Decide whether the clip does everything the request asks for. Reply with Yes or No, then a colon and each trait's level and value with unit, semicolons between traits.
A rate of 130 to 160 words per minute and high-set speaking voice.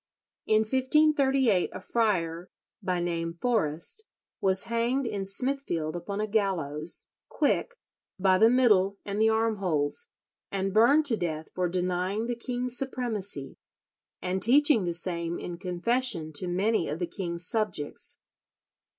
Yes: slow, 135 wpm; high, 195 Hz